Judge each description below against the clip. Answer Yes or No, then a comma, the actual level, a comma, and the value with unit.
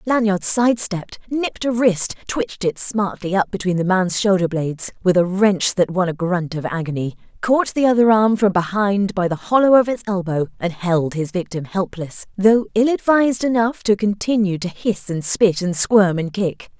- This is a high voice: Yes, high, 195 Hz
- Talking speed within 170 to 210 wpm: Yes, average, 190 wpm